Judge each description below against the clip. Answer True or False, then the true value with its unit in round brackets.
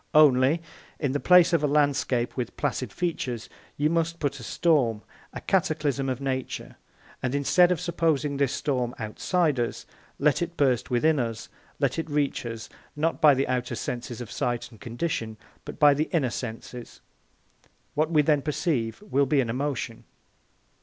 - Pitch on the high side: False (140 Hz)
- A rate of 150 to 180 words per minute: True (165 wpm)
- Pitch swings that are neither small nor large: True (4.2 semitones)